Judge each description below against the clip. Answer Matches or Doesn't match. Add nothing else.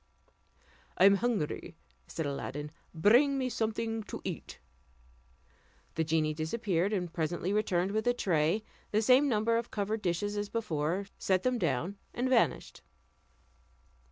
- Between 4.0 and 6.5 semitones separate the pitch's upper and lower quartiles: Matches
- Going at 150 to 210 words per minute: Doesn't match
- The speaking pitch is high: Matches